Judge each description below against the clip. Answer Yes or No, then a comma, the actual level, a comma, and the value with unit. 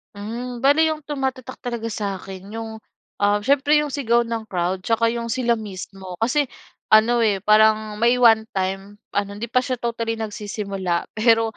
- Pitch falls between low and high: No, high, 225 Hz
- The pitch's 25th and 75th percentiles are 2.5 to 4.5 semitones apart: Yes, average, 2.9 semitones